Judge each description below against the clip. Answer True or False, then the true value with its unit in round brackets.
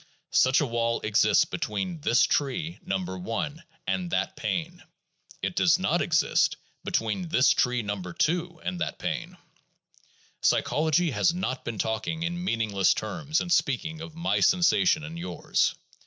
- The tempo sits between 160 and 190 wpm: False (145 wpm)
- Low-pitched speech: False (155 Hz)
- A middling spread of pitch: False (6.8 semitones)